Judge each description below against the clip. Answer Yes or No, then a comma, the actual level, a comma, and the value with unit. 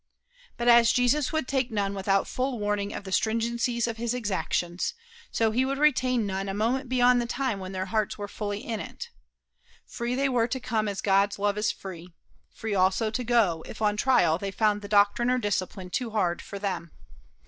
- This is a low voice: No, high, 215 Hz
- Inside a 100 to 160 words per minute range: No, fast, 205 wpm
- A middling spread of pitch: Yes, average, 3.6 semitones